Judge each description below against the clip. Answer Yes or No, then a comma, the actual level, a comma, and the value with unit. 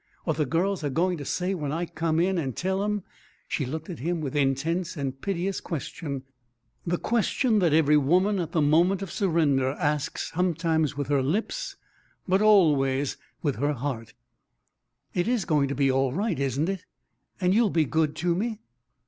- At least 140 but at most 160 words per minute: No, average, 185 wpm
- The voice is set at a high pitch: No, medium, 160 Hz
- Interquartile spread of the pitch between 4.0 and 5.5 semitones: Yes, average, 4.5 semitones